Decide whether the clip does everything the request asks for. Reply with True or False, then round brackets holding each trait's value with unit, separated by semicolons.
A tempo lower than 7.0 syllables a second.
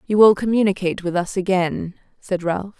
True (5.4 syllables/s)